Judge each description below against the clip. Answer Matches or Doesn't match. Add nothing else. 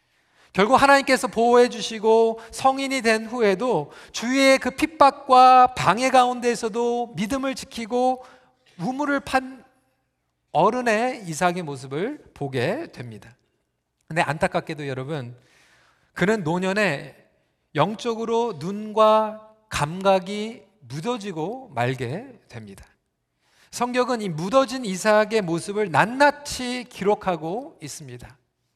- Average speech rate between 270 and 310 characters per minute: Doesn't match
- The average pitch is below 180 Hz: Doesn't match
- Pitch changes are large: Matches